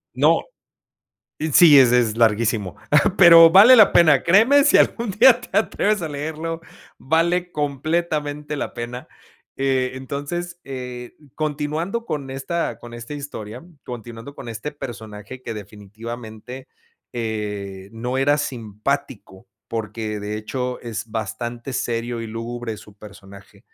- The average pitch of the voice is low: Yes, low, 125 Hz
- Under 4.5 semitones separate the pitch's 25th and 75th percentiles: No, wide, 5.4 semitones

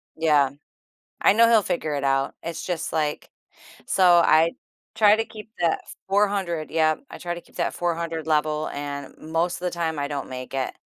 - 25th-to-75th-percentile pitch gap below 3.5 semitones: Yes, average, 3.0 semitones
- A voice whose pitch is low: No, medium, 165 Hz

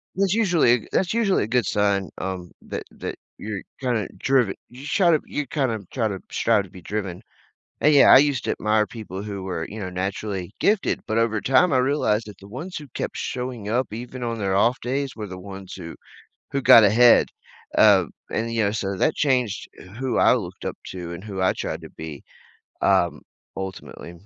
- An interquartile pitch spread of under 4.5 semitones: No, average, 5.0 semitones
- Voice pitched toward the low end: Yes, low, 110 Hz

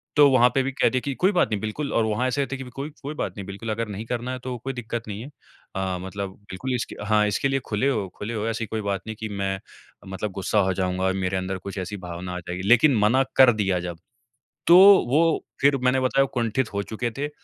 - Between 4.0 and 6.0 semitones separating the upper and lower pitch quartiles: Yes, average, 4.9 semitones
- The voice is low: Yes, low, 110 Hz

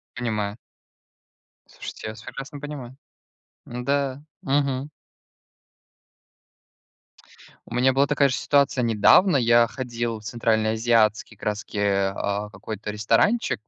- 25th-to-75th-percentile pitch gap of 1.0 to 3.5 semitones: No, average, 3.9 semitones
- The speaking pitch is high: No, low, 120 Hz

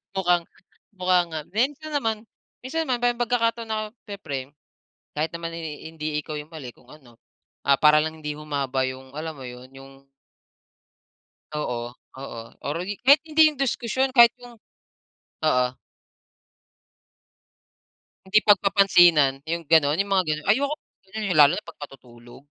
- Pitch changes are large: Yes, wide, 7.2 semitones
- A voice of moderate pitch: Yes, medium, 165 Hz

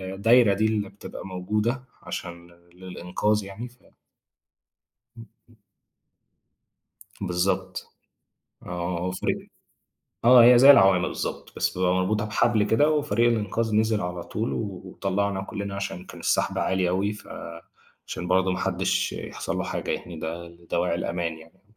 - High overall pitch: No, very low, 95 Hz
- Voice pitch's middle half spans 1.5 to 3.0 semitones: No, average, 3.5 semitones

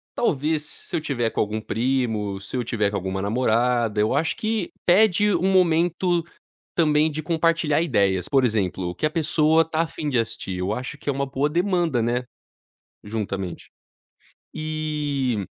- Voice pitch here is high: No, medium, 140 Hz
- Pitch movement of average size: No, wide, 6.7 semitones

